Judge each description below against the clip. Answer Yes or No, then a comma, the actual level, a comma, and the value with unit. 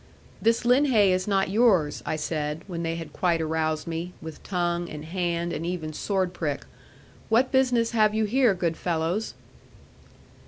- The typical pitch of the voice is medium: Yes, medium, 175 Hz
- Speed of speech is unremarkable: Yes, average, 160 wpm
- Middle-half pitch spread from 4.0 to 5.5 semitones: Yes, average, 4.8 semitones